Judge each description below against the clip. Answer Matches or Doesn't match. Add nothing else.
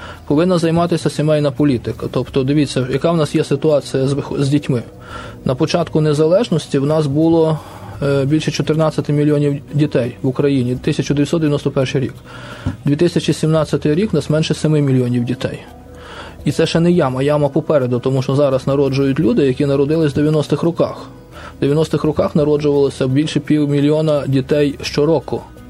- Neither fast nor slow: Matches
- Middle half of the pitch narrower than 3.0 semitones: Matches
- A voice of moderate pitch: Matches